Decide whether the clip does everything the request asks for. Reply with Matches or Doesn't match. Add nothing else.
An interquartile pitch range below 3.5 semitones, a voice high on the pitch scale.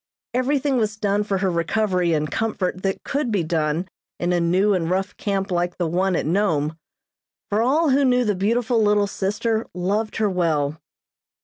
Doesn't match